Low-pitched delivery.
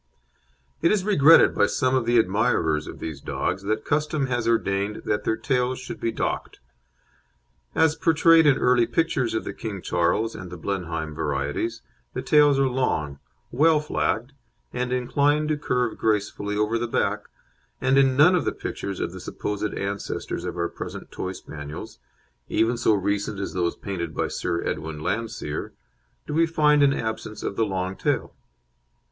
Yes: low, 115 Hz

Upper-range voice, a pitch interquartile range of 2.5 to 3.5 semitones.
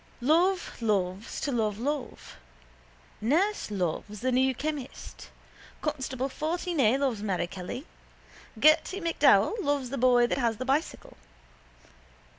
No: very high, 260 Hz; wide, 5.5 semitones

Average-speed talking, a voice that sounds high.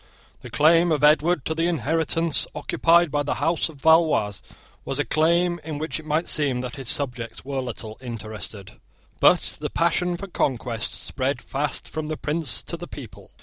No: average, 180 wpm; medium, 150 Hz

